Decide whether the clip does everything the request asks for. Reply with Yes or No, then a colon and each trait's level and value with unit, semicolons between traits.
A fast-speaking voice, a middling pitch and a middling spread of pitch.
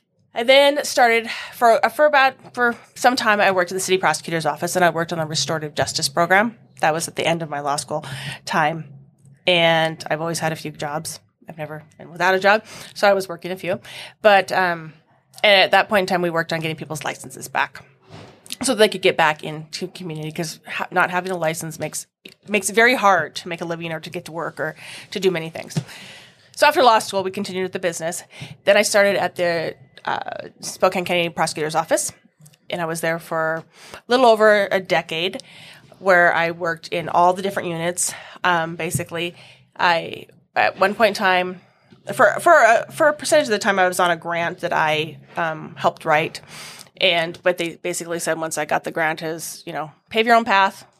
Yes: fast, 215 wpm; medium, 175 Hz; average, 3.4 semitones